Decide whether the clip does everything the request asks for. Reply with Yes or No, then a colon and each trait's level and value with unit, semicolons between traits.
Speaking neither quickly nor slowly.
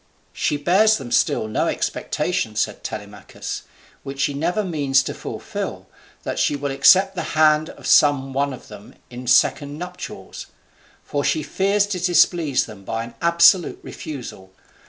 Yes: average, 155 wpm